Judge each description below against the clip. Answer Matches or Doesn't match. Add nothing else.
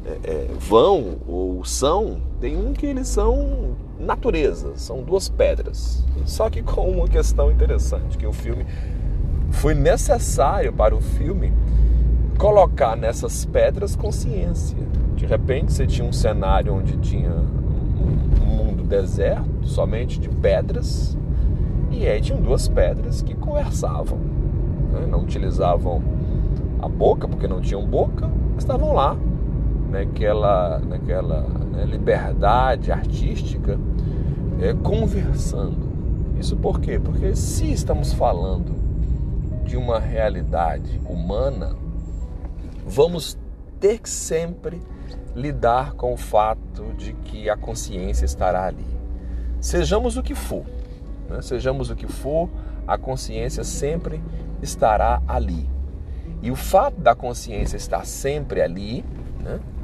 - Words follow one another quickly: Doesn't match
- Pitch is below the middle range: Matches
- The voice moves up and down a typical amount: Doesn't match